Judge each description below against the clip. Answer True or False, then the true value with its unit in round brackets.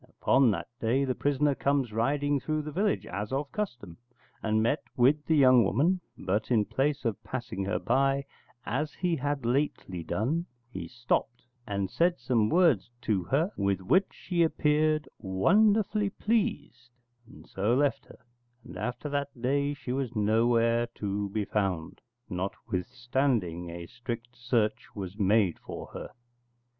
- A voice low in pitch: True (125 Hz)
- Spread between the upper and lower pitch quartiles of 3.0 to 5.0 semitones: False (5.6 semitones)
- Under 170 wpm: True (150 wpm)